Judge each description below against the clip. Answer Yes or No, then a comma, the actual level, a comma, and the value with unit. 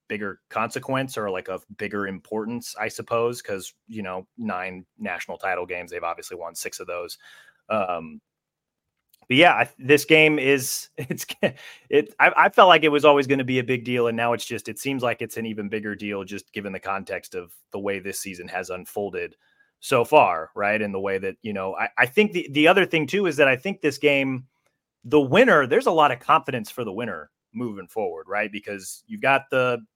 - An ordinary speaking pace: No, fast, 215 wpm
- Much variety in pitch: Yes, wide, 6.7 semitones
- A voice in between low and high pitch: No, low, 125 Hz